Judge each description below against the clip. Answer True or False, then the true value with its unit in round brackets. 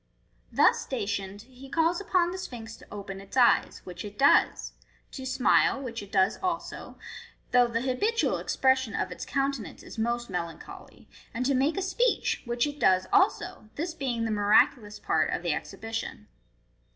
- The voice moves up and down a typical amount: True (5.0 semitones)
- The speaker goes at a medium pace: True (170 wpm)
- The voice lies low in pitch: False (245 Hz)